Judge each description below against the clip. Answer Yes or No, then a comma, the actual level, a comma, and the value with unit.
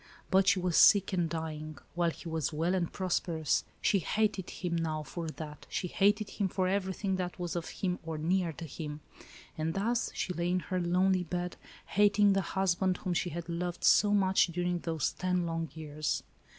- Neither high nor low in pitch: Yes, medium, 175 Hz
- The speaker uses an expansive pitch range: No, narrow, 2.5 semitones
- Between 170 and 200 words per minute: Yes, average, 190 wpm